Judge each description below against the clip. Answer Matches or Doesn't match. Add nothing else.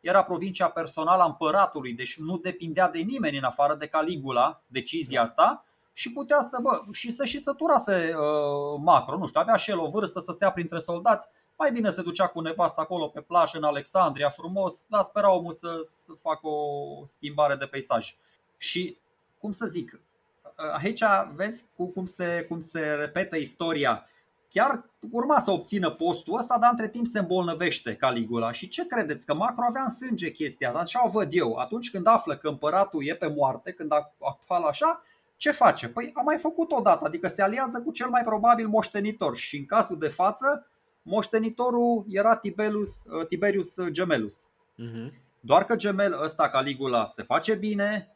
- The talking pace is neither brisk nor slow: Doesn't match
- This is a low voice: Doesn't match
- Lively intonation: Matches